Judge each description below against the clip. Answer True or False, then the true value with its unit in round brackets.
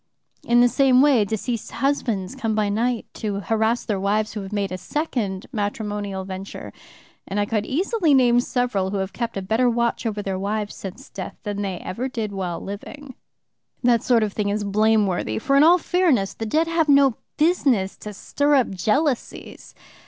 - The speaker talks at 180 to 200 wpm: True (185 wpm)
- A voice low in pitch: False (220 Hz)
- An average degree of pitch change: True (4.4 semitones)